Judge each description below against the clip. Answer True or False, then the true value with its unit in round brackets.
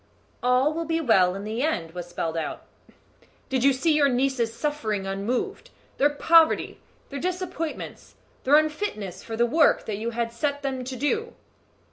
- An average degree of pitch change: False (5.7 semitones)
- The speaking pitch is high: True (260 Hz)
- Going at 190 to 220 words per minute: False (165 wpm)